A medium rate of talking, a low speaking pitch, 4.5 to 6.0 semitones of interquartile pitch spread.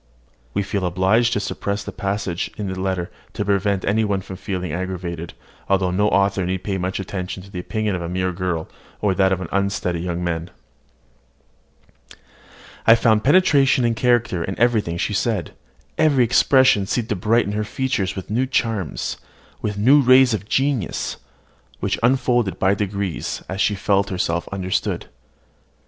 No: average, 165 wpm; low, 100 Hz; average, 3.4 semitones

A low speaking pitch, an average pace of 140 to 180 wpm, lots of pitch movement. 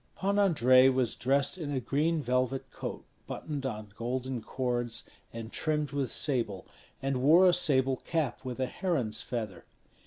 No: low, 130 Hz; average, 155 wpm; average, 3.6 semitones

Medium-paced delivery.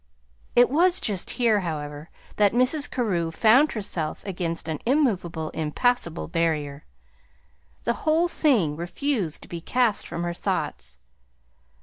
No: slow, 125 wpm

